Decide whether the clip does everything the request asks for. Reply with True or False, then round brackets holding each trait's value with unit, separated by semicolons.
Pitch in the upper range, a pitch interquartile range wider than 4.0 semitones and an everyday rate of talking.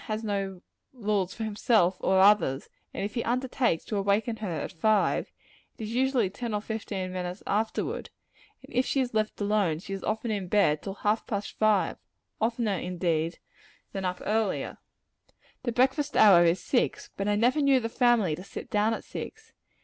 False (210 Hz; 3.2 semitones; 180 wpm)